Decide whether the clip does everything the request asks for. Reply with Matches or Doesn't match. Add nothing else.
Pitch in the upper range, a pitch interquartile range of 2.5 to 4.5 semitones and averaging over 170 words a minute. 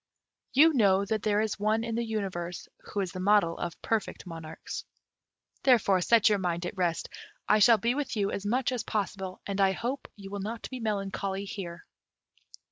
Matches